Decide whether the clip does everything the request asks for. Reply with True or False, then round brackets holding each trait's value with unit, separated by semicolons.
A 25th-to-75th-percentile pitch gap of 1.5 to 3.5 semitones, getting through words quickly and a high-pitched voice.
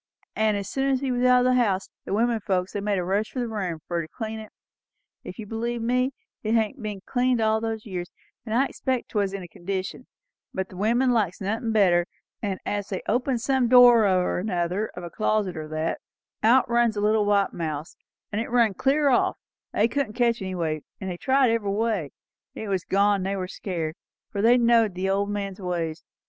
False (3.9 semitones; 225 wpm; 210 Hz)